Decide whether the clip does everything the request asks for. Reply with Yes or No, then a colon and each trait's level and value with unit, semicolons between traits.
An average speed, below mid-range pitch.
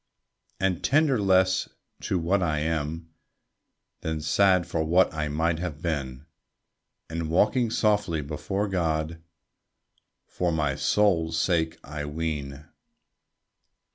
No: slow, 110 wpm; very low, 80 Hz